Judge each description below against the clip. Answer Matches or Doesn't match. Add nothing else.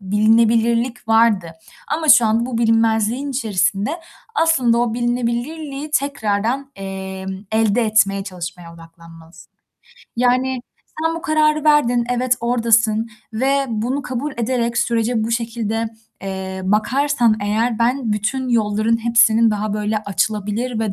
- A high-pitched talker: Matches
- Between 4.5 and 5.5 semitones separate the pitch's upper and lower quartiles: Doesn't match